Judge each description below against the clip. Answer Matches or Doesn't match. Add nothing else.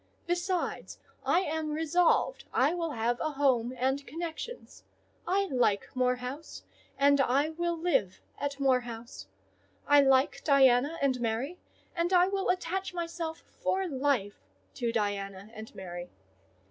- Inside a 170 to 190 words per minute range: Doesn't match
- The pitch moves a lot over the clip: Matches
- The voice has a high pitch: Matches